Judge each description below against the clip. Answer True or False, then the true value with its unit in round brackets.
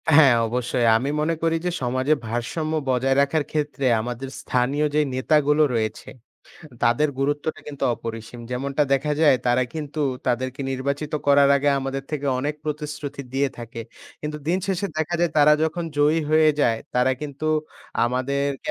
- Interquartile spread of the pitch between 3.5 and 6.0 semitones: False (3.1 semitones)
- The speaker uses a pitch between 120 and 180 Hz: True (140 Hz)